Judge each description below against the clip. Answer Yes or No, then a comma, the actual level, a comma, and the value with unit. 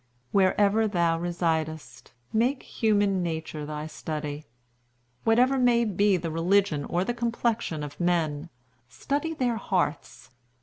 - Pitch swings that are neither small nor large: No, wide, 5.9 semitones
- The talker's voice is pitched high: No, medium, 180 Hz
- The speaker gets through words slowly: Yes, slow, 120 wpm